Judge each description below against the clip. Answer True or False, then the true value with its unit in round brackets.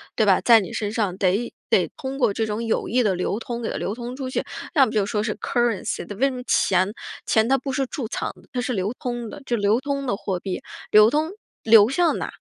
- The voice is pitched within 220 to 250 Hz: True (230 Hz)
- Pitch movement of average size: True (3.7 semitones)